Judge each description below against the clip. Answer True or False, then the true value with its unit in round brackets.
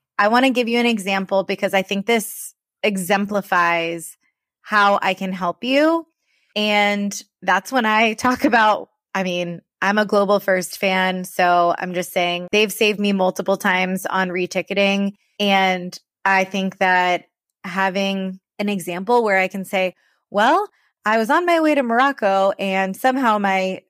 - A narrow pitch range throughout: True (2.2 semitones)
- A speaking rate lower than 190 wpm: True (160 wpm)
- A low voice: False (195 Hz)